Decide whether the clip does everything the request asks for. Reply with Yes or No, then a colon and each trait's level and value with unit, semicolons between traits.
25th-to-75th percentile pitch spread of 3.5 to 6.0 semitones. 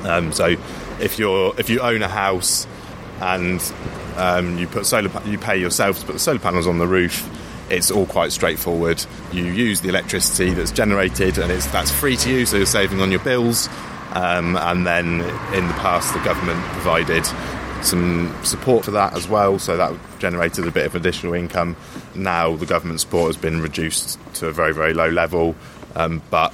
No: narrow, 2.4 semitones